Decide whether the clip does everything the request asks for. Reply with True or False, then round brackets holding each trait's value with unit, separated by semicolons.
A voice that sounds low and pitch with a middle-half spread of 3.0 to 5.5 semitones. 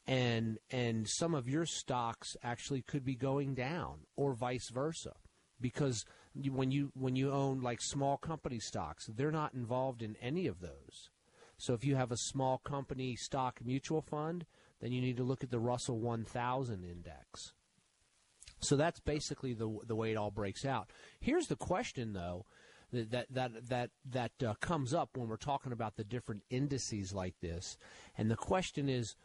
True (125 Hz; 3.5 semitones)